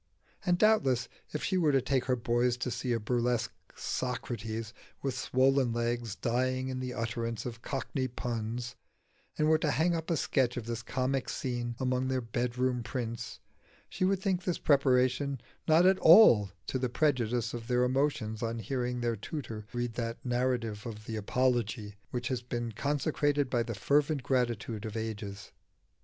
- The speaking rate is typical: Yes, average, 170 wpm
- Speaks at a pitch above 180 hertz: No, low, 125 Hz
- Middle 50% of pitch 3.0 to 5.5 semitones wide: No, narrow, 2.5 semitones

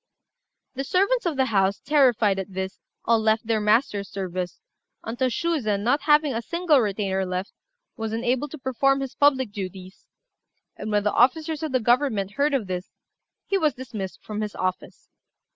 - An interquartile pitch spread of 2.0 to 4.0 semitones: No, wide, 5.6 semitones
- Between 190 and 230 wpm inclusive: No, average, 170 wpm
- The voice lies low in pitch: No, high, 230 Hz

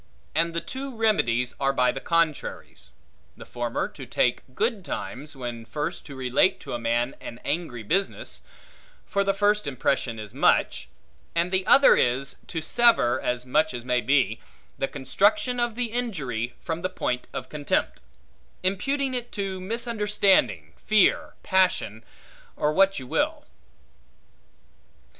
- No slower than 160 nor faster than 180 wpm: No, average, 145 wpm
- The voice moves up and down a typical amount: No, wide, 8.3 semitones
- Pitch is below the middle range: No, medium, 155 Hz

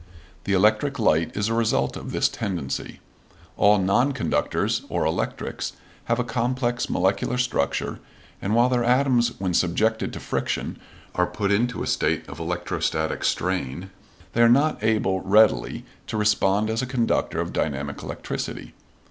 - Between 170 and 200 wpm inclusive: No, average, 150 wpm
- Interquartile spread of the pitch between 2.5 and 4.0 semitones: No, average, 4.6 semitones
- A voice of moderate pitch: No, low, 105 Hz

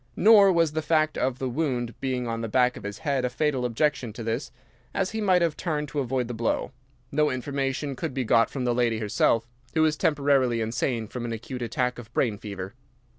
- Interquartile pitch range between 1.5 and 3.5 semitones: No, average, 4.2 semitones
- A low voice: Yes, low, 130 Hz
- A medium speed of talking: No, fast, 220 wpm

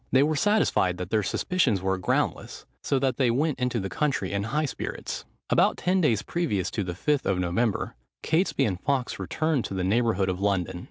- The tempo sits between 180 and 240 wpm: Yes, average, 200 wpm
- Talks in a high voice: No, low, 115 Hz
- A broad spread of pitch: Yes, wide, 7.3 semitones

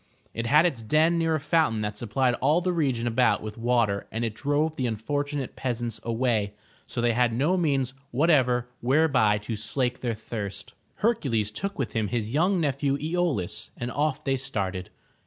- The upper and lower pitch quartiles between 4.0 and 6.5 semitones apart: Yes, average, 4.6 semitones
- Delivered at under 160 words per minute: No, average, 180 wpm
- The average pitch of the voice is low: Yes, low, 125 Hz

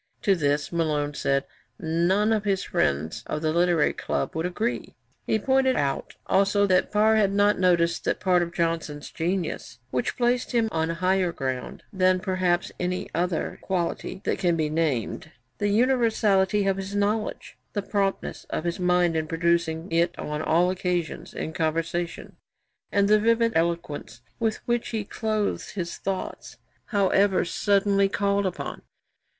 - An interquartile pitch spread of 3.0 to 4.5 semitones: Yes, average, 3.6 semitones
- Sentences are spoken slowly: No, average, 155 wpm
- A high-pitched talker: No, medium, 180 Hz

